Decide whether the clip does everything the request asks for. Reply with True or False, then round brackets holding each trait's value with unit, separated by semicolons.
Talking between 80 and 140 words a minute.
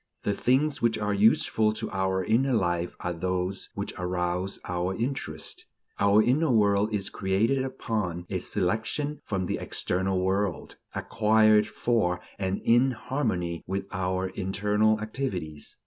True (135 wpm)